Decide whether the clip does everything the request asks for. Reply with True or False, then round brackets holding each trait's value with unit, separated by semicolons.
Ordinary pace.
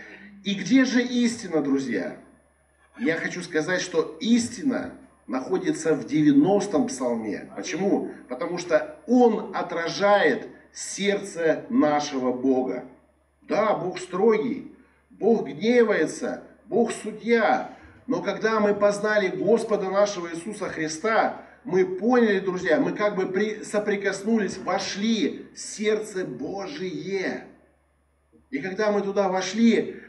False (105 wpm)